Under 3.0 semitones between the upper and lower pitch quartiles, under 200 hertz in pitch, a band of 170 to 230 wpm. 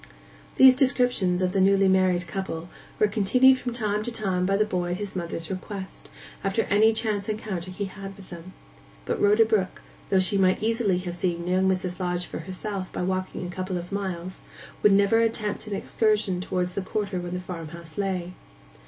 Yes: narrow, 2.5 semitones; high, 190 Hz; average, 195 wpm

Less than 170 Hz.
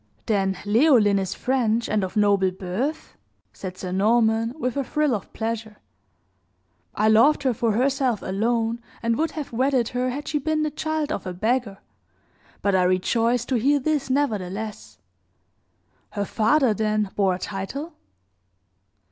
No: high, 230 Hz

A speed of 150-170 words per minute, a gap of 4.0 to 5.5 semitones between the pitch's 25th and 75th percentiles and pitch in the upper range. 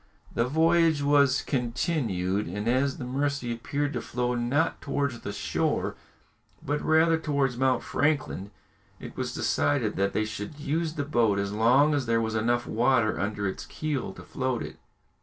No: average, 165 wpm; average, 4.5 semitones; low, 130 Hz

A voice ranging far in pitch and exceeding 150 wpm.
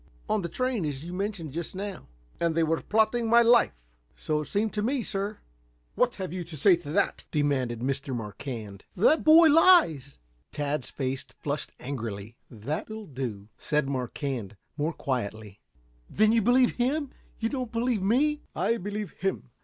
Yes: wide, 8.8 semitones; average, 170 wpm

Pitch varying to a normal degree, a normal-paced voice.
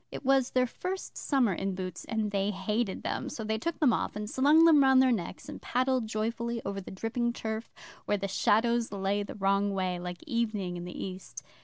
No: average, 4.1 semitones; fast, 210 wpm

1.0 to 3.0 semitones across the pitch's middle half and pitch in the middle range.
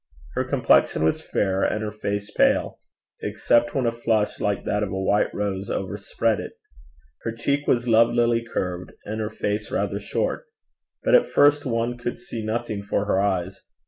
No: average, 2.7 semitones; low, 110 Hz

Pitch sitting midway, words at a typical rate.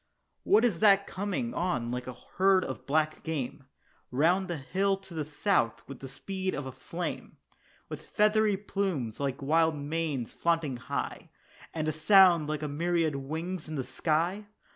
Yes: medium, 160 Hz; average, 165 wpm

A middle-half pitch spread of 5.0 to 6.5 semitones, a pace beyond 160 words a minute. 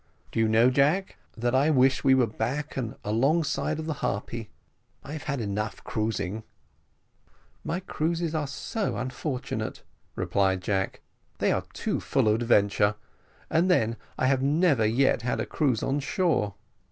No: wide, 5.4 semitones; average, 155 wpm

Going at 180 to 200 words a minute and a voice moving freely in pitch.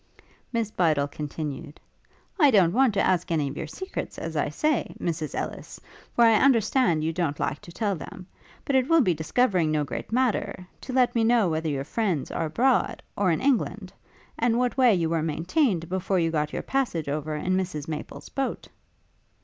Yes: average, 190 wpm; wide, 7.2 semitones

